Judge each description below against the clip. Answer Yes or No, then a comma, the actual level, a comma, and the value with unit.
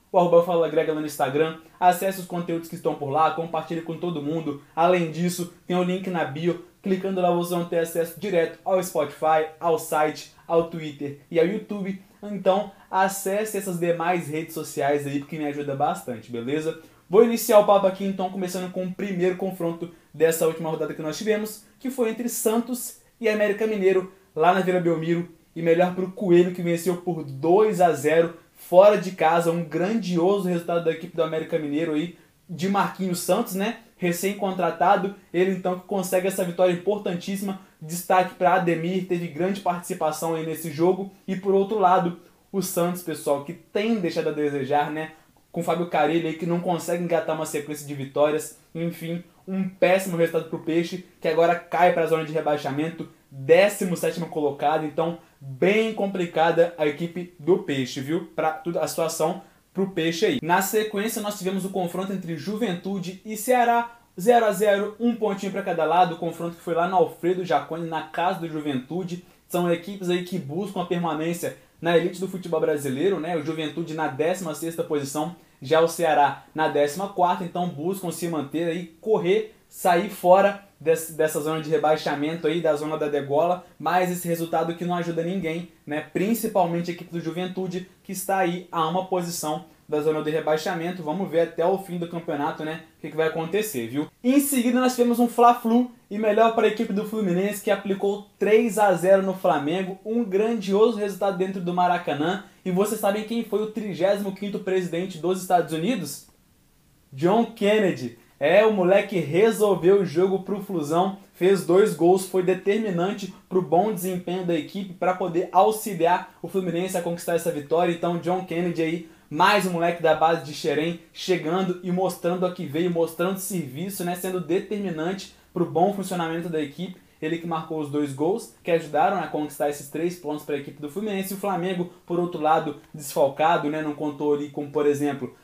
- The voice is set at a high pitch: No, medium, 175 Hz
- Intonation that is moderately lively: Yes, average, 3.0 semitones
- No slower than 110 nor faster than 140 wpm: No, fast, 185 wpm